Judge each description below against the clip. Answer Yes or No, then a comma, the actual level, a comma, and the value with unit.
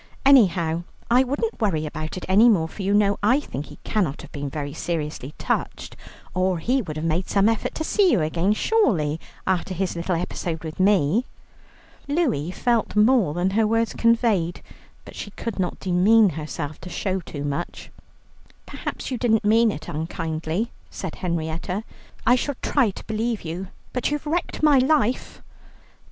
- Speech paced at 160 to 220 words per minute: Yes, average, 170 wpm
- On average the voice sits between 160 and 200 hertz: Yes, high, 190 Hz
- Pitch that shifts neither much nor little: No, wide, 6.0 semitones